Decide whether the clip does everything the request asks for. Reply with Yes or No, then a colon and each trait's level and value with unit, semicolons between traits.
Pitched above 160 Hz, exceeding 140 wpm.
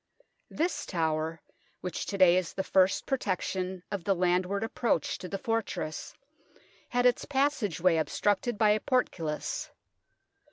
No: high, 190 Hz; slow, 135 wpm